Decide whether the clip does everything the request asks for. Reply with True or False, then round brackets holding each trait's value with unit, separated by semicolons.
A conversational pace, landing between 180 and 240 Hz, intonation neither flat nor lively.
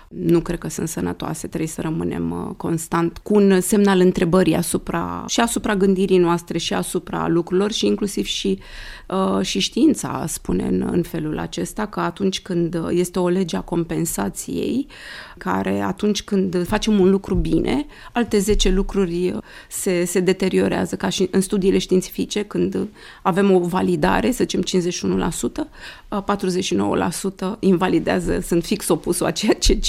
False (145 wpm; 185 Hz; 2.3 semitones)